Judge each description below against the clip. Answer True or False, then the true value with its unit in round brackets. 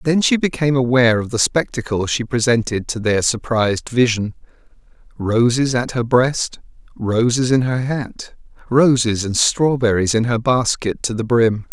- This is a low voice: True (120 Hz)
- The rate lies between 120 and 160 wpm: True (155 wpm)